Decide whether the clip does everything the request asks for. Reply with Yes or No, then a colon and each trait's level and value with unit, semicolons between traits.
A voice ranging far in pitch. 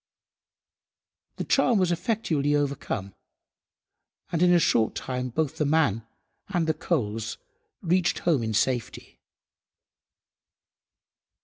Yes: wide, 6.7 semitones